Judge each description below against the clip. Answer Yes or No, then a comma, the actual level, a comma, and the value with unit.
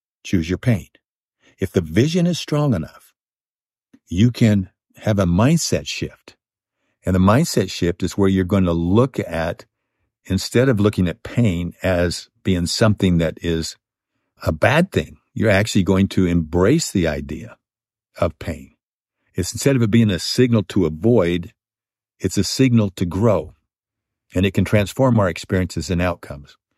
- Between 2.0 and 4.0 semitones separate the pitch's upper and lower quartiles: No, average, 4.6 semitones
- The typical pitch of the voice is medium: No, very low, 95 Hz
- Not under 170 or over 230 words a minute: No, average, 155 wpm